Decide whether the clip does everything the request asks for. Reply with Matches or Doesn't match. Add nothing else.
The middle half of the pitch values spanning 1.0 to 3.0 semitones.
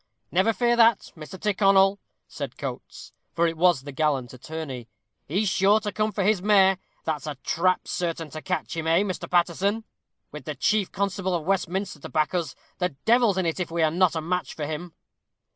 Doesn't match